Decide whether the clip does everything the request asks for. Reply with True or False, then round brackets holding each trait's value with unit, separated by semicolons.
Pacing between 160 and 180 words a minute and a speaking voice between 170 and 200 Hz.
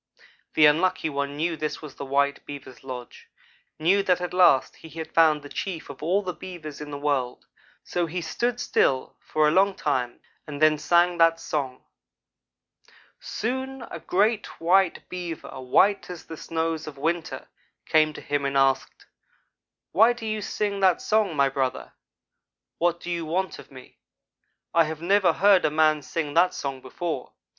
False (170 wpm; 160 Hz)